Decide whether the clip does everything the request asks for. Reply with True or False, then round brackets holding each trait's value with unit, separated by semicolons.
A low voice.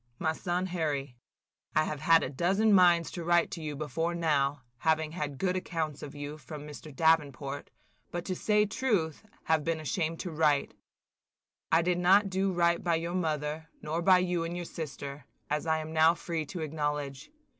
False (160 Hz)